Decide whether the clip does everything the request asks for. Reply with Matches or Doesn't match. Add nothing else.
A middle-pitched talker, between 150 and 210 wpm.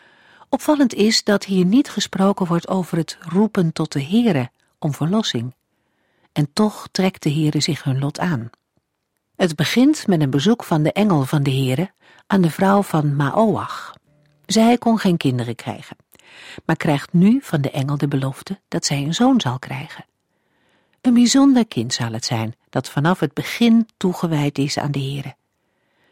Matches